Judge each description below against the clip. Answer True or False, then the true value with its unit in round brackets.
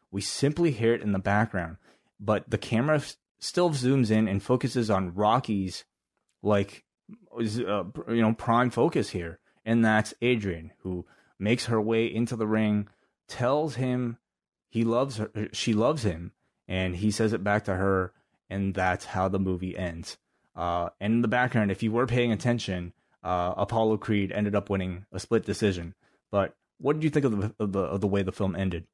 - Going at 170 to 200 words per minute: True (185 wpm)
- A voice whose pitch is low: True (105 Hz)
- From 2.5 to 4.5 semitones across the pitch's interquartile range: True (3.4 semitones)